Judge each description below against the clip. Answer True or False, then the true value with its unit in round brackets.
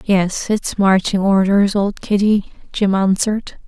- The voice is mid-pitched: False (200 Hz)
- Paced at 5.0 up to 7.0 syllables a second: False (3.9 syllables/s)